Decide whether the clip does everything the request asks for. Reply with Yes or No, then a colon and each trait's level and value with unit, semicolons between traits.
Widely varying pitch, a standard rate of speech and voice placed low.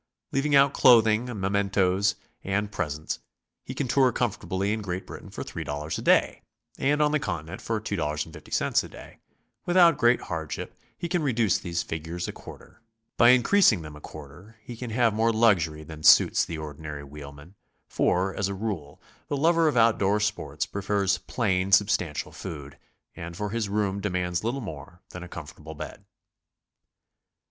Yes: wide, 6.1 semitones; average, 165 wpm; low, 100 Hz